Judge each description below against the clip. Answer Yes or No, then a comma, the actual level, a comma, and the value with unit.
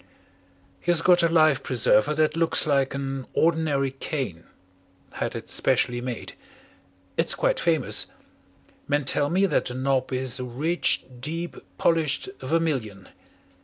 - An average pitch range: Yes, average, 4.1 semitones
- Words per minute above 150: No, slow, 135 wpm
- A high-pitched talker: No, medium, 145 Hz